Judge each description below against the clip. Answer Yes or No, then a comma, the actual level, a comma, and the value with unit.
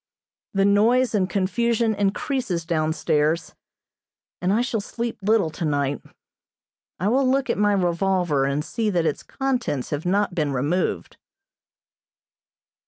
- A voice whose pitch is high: Yes, high, 195 Hz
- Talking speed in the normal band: No, slow, 130 wpm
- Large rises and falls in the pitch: Yes, wide, 6.0 semitones